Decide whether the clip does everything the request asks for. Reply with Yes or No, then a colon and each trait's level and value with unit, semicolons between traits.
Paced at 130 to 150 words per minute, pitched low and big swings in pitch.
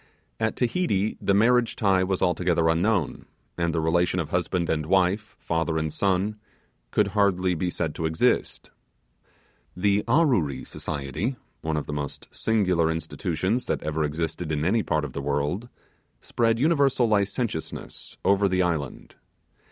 No: average, 145 wpm; very low, 90 Hz; average, 4.6 semitones